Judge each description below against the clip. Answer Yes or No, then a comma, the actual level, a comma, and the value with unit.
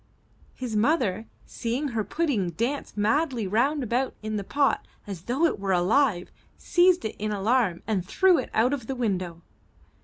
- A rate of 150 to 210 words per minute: Yes, average, 165 wpm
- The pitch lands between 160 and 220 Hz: No, high, 230 Hz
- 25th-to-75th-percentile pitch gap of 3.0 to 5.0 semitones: No, wide, 5.5 semitones